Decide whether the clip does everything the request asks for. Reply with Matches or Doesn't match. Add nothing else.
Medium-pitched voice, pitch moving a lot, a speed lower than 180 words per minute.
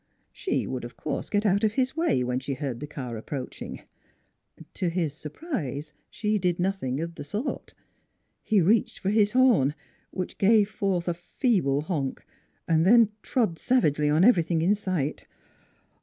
Matches